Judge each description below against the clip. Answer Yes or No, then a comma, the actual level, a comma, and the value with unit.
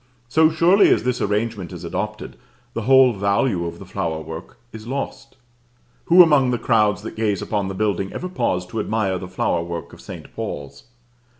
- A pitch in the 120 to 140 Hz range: No, low, 105 Hz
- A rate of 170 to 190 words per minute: Yes, average, 185 wpm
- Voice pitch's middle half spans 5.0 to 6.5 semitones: Yes, wide, 5.4 semitones